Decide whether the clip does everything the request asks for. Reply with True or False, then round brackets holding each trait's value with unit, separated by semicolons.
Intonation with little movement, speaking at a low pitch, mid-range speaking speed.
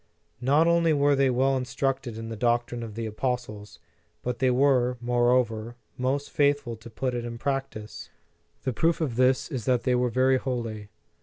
True (2.3 semitones; 125 Hz; 180 wpm)